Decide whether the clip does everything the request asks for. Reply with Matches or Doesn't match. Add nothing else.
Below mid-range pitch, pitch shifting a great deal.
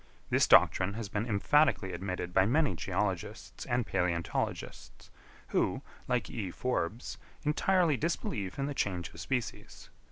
Matches